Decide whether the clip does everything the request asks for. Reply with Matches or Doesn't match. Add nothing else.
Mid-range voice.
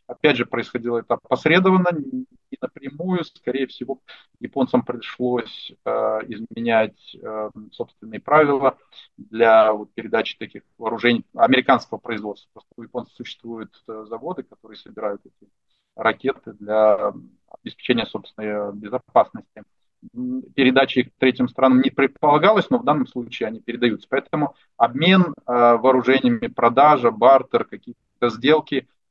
Doesn't match